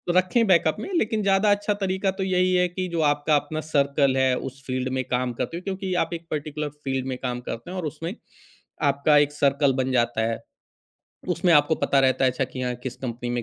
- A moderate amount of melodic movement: No, wide, 5.7 semitones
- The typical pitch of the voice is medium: Yes, medium, 145 Hz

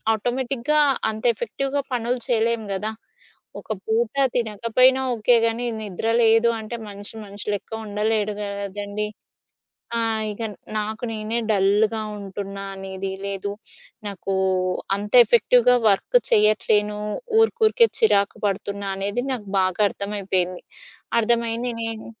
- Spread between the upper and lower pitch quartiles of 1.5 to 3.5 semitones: Yes, average, 2.7 semitones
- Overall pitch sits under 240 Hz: Yes, high, 215 Hz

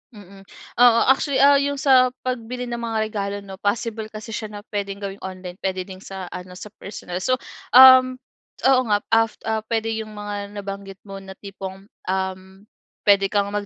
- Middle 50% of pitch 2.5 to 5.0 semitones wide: Yes, average, 3.3 semitones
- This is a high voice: Yes, high, 205 Hz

